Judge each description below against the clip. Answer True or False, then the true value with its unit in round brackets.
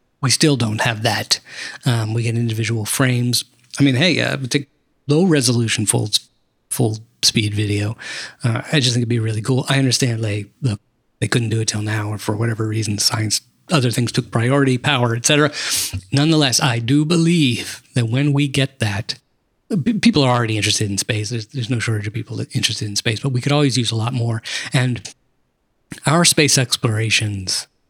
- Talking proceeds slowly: False (190 wpm)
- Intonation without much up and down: False (3.6 semitones)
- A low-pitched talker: True (120 Hz)